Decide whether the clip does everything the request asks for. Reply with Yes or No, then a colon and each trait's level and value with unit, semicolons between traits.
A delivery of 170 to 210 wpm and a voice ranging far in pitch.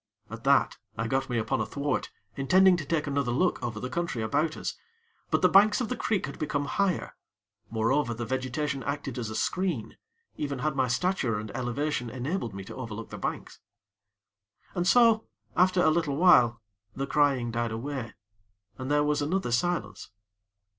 Yes: average, 175 wpm; wide, 6.0 semitones